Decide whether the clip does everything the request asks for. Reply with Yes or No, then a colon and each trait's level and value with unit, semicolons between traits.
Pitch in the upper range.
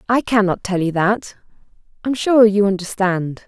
Yes: high, 205 Hz